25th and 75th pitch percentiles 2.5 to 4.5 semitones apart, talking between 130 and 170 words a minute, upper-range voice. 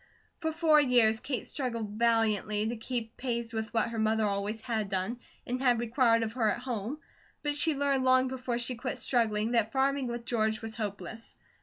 No: average, 2.8 semitones; average, 190 wpm; high, 235 Hz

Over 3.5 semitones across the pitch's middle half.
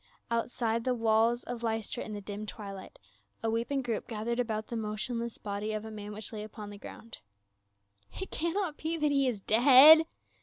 No: narrow, 2.6 semitones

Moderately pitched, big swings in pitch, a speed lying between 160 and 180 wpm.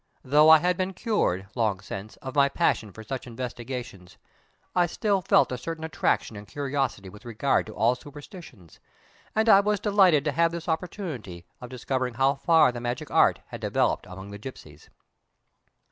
No: low, 130 Hz; wide, 6.9 semitones; average, 175 wpm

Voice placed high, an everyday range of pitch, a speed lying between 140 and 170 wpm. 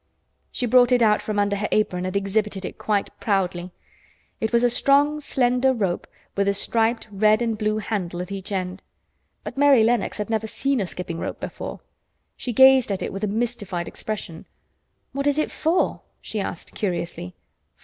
No: high, 215 Hz; average, 3.9 semitones; average, 180 wpm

